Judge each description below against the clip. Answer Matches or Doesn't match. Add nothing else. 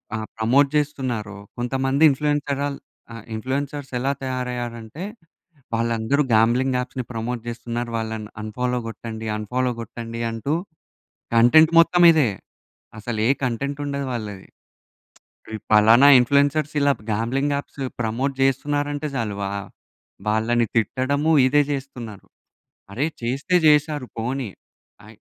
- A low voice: Matches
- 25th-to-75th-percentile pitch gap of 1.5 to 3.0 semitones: Doesn't match